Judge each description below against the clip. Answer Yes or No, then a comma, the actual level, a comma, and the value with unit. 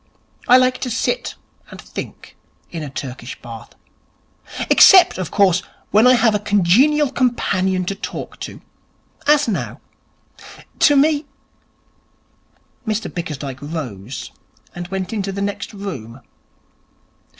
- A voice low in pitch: No, high, 195 Hz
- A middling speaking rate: No, slow, 125 wpm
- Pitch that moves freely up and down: Yes, wide, 7.7 semitones